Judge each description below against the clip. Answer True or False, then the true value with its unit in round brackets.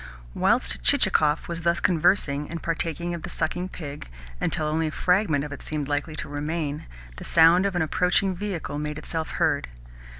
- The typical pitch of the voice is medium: True (160 Hz)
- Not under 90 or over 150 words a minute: False (175 wpm)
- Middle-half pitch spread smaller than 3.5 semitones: True (2.7 semitones)